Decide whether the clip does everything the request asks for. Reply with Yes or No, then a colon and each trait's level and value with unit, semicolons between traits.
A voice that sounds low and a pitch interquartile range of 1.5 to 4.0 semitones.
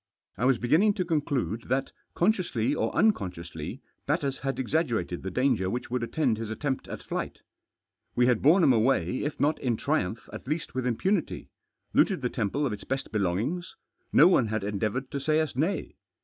No: low, 130 Hz; wide, 5.5 semitones